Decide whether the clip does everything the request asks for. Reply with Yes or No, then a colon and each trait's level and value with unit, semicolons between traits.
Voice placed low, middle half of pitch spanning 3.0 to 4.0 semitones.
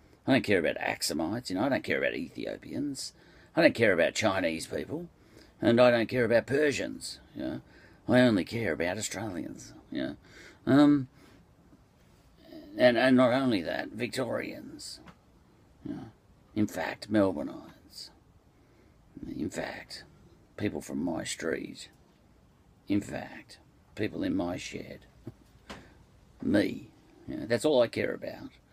No: low, 125 Hz; average, 5.1 semitones